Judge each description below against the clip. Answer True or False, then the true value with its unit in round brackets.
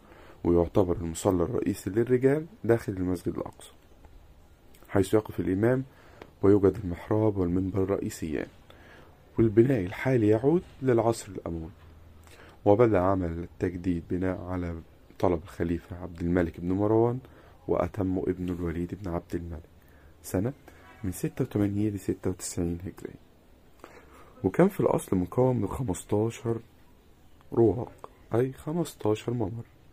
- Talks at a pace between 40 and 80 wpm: False (105 wpm)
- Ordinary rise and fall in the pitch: True (4.3 semitones)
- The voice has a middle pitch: False (95 Hz)